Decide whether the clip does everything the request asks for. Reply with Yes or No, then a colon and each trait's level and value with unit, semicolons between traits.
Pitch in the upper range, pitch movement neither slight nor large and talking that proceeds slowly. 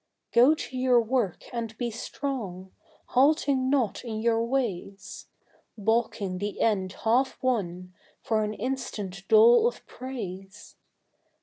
Yes: high, 230 Hz; average, 4.6 semitones; slow, 120 wpm